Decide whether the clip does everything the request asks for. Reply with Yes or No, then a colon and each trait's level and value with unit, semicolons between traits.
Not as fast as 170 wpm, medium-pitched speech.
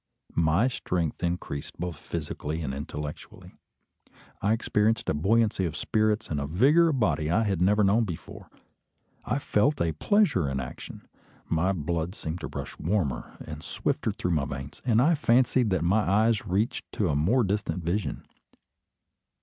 No: average, 160 wpm; very low, 95 Hz